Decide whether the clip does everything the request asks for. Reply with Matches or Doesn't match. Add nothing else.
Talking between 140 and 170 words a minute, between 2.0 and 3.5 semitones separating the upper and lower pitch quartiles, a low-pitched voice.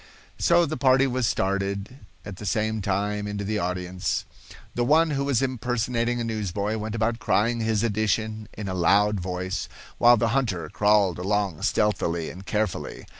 Matches